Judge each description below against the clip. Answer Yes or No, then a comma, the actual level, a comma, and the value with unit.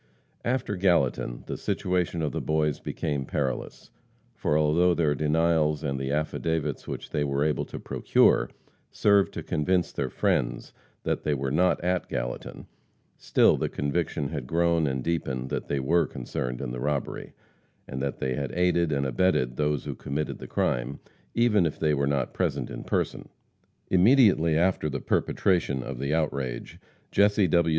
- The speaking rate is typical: Yes, average, 165 wpm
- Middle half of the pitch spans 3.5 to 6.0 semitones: Yes, average, 3.9 semitones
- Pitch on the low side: Yes, very low, 75 Hz